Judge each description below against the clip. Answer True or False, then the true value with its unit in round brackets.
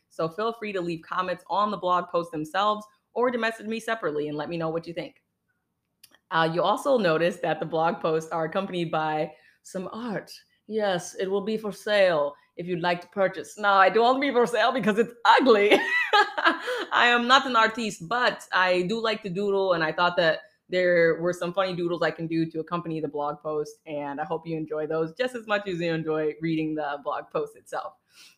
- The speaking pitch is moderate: True (180 Hz)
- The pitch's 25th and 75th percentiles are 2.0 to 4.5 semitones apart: False (5.1 semitones)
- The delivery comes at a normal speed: False (215 wpm)